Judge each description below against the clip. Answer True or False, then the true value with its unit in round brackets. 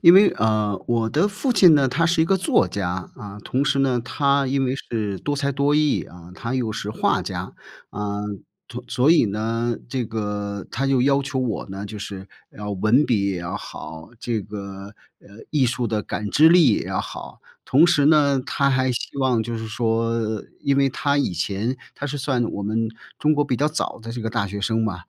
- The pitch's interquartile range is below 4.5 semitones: False (5.3 semitones)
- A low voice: True (120 Hz)